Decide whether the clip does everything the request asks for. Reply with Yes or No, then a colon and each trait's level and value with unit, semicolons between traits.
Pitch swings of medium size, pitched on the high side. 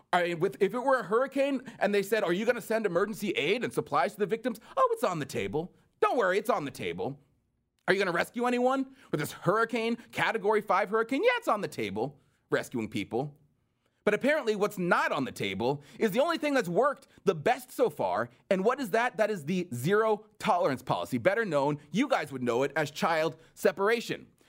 No: wide, 6.2 semitones; high, 210 Hz